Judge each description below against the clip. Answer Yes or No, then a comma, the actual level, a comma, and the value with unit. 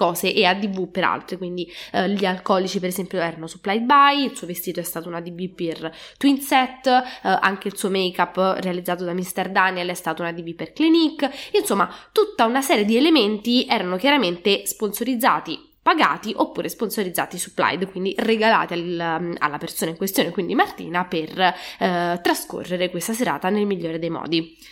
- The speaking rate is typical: Yes, average, 170 wpm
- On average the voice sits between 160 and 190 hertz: Yes, medium, 185 Hz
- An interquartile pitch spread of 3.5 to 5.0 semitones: Yes, average, 4.4 semitones